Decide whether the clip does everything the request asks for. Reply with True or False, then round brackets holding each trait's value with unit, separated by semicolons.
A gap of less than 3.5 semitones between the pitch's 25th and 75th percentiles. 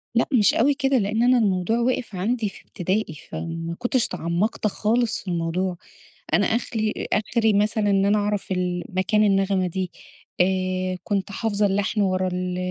True (3.0 semitones)